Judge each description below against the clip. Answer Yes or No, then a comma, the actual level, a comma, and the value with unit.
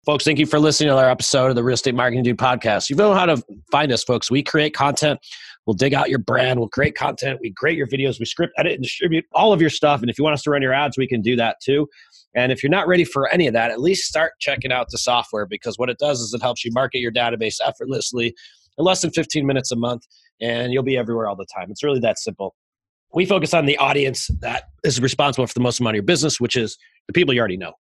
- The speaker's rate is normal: No, fast, 280 wpm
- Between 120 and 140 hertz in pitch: Yes, low, 130 Hz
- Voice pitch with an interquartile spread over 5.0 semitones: No, average, 3.5 semitones